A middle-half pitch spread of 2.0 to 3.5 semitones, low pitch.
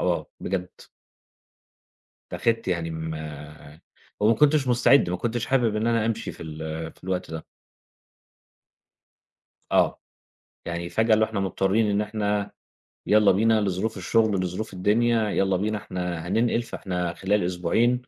No: average, 4.2 semitones; low, 100 Hz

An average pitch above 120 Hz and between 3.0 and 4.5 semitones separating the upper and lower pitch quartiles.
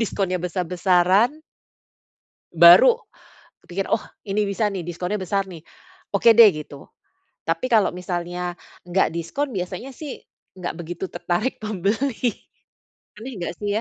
Yes: high, 190 Hz; average, 3.7 semitones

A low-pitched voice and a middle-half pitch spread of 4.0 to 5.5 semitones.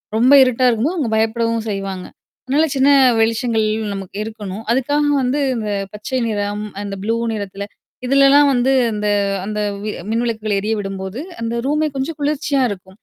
No: high, 225 Hz; average, 4.3 semitones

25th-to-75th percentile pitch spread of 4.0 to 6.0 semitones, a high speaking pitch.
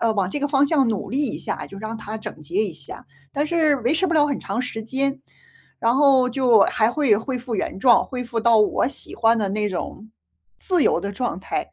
Yes: average, 4.4 semitones; high, 235 Hz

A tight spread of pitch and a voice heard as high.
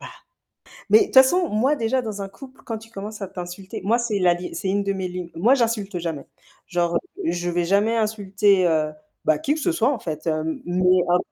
No: average, 4.5 semitones; high, 195 Hz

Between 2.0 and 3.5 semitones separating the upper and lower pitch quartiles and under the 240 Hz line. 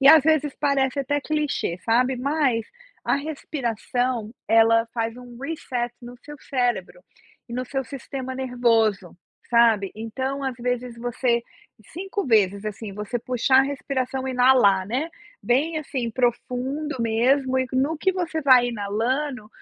No: average, 3.0 semitones; very high, 250 Hz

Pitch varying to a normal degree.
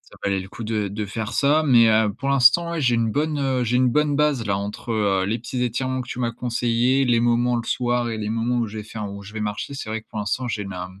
Yes: average, 3.1 semitones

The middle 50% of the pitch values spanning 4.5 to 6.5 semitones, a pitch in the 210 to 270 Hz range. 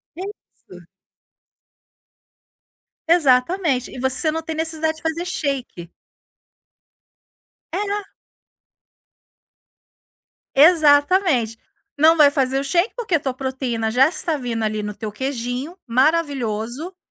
No: average, 4.8 semitones; very high, 280 Hz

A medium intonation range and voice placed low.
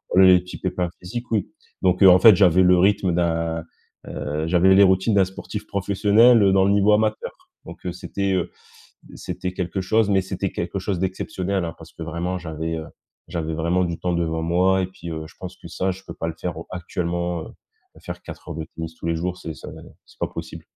No: narrow, 2.2 semitones; very low, 90 Hz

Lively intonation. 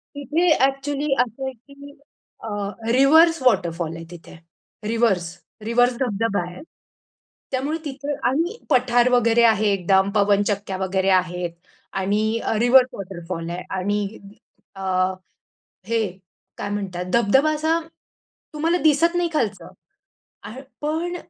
Yes: wide, 6.3 semitones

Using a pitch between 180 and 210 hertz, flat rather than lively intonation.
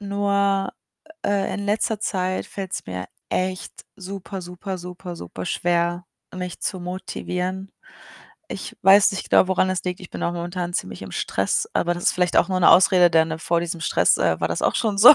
Yes: medium, 185 Hz; narrow, 2.0 semitones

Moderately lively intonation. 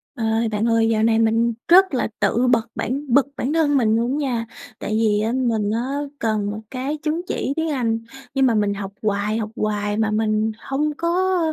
Yes: average, 3.9 semitones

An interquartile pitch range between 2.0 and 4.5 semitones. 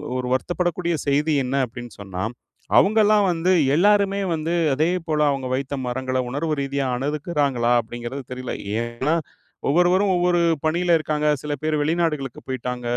No: average, 5.1 semitones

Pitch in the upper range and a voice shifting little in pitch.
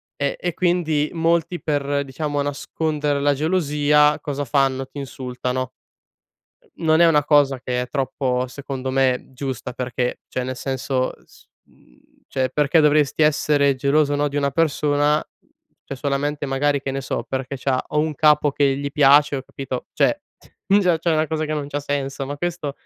No: medium, 145 Hz; narrow, 1.9 semitones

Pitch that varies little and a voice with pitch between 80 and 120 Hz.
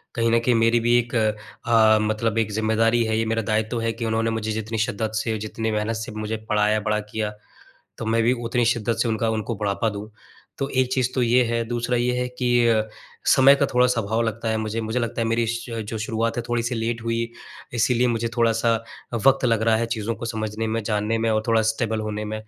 Yes: narrow, 1.3 semitones; low, 115 Hz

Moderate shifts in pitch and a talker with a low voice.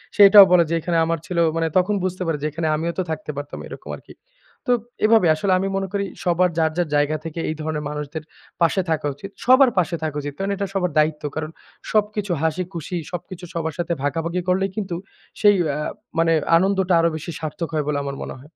No: average, 3.3 semitones; medium, 170 Hz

